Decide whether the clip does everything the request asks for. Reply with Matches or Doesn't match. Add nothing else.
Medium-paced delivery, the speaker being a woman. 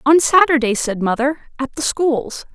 Matches